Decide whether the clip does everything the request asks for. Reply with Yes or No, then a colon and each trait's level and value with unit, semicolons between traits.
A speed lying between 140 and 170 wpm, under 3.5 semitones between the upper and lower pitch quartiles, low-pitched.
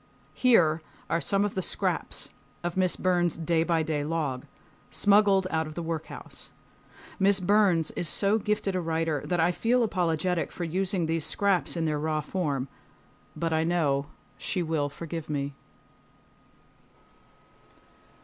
No: average, 145 wpm; average, 2.9 semitones; medium, 165 Hz